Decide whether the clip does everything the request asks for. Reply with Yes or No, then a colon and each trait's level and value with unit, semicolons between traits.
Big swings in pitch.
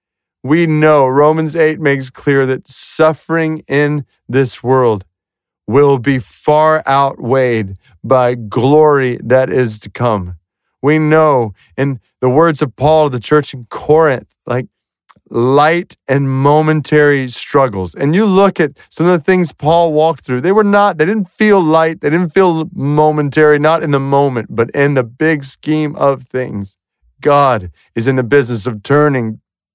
No: average, 3.6 semitones